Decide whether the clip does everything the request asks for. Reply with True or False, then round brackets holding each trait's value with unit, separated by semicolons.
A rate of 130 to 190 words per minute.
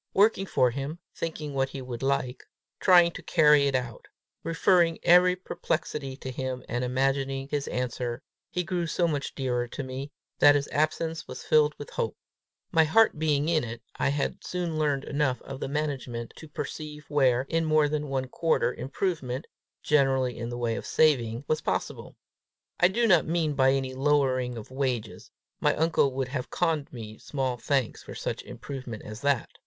True (180 wpm)